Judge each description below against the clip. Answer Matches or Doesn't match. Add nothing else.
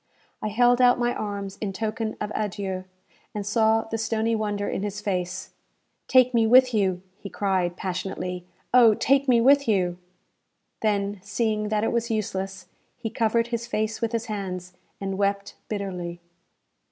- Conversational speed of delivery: Matches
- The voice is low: Doesn't match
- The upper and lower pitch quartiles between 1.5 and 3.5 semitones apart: Matches